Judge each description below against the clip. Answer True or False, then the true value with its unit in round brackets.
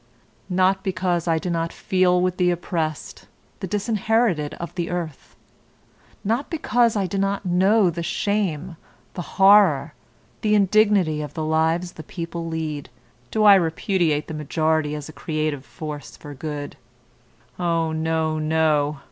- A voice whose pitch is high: False (170 Hz)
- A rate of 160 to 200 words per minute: False (145 wpm)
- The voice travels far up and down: False (3.6 semitones)